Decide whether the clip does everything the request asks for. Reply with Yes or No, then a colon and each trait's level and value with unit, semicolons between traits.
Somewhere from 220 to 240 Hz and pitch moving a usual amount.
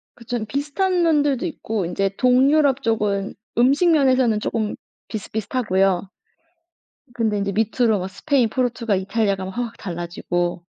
Yes: high, 225 Hz; average, 4.9 semitones